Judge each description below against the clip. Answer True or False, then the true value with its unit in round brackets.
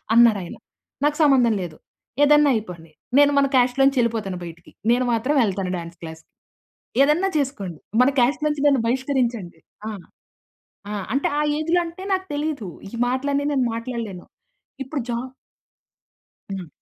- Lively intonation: True (6.5 semitones)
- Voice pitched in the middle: False (250 Hz)